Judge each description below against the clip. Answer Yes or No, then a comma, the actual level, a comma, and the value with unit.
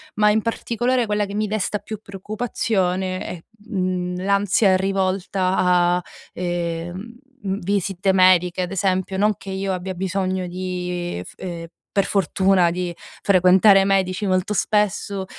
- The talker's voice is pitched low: No, high, 190 Hz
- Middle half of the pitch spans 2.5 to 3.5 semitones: No, narrow, 1.8 semitones